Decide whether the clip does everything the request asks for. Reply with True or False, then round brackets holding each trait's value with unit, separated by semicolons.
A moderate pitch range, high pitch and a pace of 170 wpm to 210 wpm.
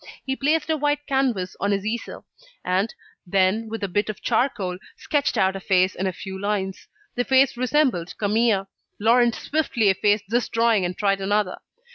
True (4.3 semitones; 210 Hz; 175 wpm)